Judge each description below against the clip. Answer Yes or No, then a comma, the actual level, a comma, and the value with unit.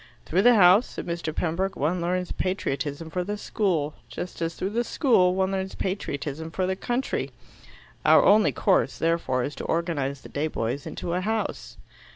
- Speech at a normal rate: Yes, average, 180 wpm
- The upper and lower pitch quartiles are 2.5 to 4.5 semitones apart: Yes, average, 3.4 semitones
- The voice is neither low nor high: Yes, medium, 180 Hz